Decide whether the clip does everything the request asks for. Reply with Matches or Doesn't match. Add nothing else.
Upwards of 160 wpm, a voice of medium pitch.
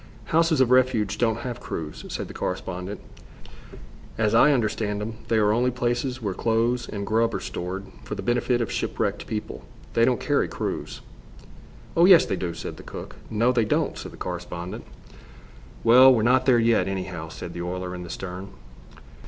Doesn't match